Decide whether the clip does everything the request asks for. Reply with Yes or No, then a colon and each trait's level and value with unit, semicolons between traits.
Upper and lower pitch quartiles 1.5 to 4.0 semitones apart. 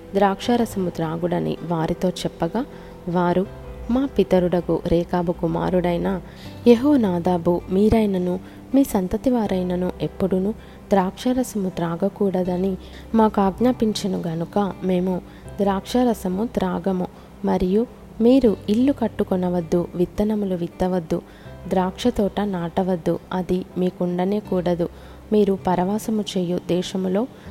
Yes: average, 2.7 semitones